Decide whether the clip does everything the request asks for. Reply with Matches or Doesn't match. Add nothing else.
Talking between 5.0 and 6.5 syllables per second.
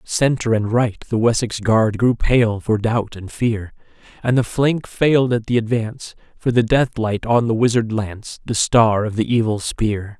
Doesn't match